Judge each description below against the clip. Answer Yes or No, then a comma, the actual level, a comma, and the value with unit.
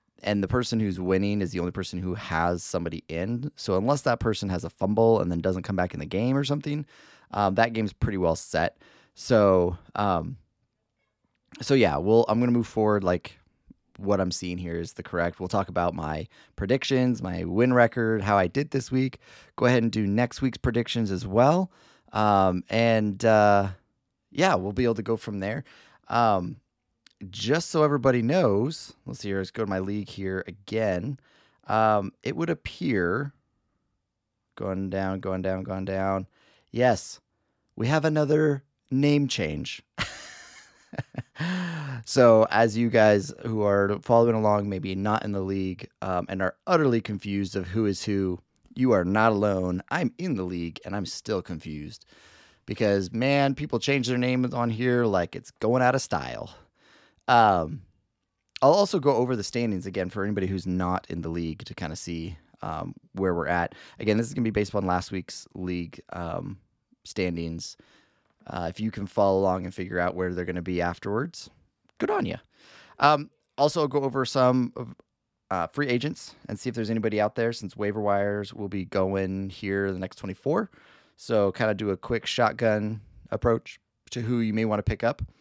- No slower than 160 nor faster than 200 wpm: Yes, average, 185 wpm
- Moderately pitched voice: No, low, 105 Hz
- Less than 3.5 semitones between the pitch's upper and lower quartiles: No, average, 4.1 semitones